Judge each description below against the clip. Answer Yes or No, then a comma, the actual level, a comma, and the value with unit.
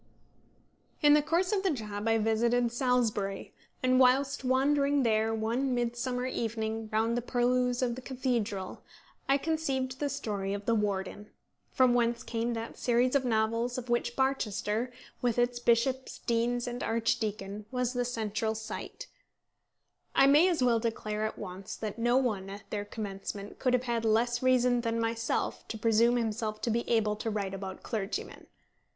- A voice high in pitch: Yes, high, 235 Hz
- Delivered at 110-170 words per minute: Yes, average, 165 wpm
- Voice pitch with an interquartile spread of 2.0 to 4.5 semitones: Yes, narrow, 2.5 semitones